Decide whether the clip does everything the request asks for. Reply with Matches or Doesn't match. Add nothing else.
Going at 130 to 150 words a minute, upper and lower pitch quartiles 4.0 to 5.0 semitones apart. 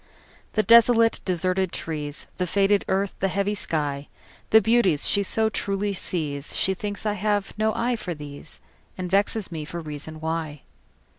Matches